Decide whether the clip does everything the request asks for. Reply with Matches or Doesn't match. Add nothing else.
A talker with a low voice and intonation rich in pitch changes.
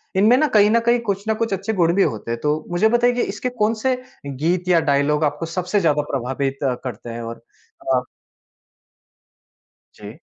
Doesn't match